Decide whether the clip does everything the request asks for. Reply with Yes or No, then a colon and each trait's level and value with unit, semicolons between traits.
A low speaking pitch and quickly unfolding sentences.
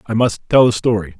Yes: low, 110 Hz; fast, 250 wpm